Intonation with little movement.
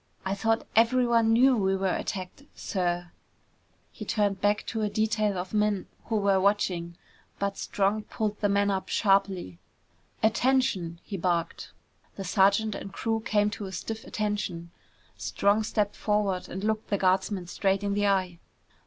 Yes: narrow, 2.2 semitones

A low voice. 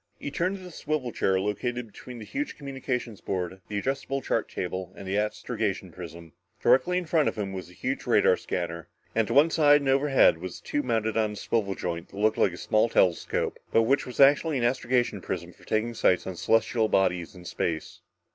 Yes: low, 110 Hz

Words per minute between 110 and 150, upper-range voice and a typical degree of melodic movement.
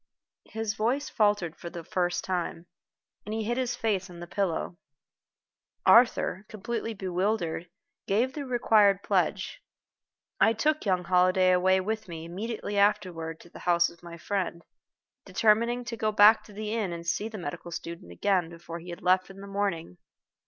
No: average, 170 wpm; high, 195 Hz; average, 4.1 semitones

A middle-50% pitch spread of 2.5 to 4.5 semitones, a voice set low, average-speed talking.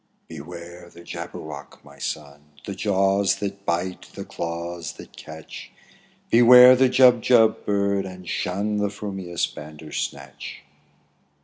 No: average, 3.7 semitones; very low, 95 Hz; slow, 120 wpm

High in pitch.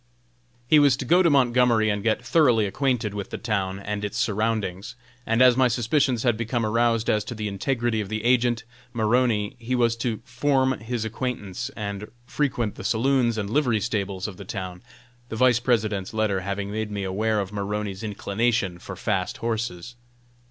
No: low, 110 Hz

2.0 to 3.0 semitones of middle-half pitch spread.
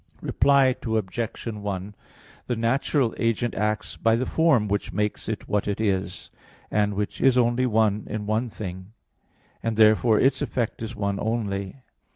Yes: narrow, 2.6 semitones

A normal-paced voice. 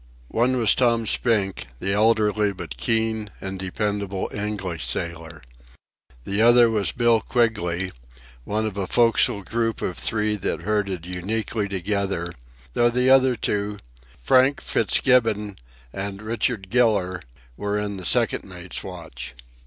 No: slow, 130 wpm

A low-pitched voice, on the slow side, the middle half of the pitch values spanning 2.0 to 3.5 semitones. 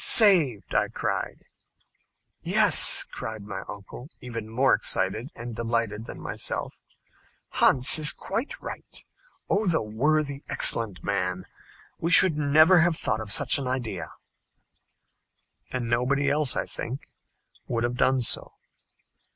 No: low, 125 Hz; slow, 125 wpm; average, 5.1 semitones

